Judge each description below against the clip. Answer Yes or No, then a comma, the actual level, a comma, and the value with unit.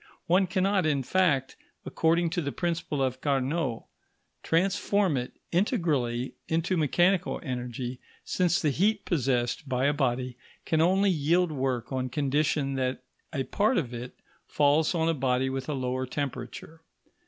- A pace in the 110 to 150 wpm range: Yes, average, 145 wpm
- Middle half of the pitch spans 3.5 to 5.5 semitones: Yes, average, 5.0 semitones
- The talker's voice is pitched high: No, medium, 145 Hz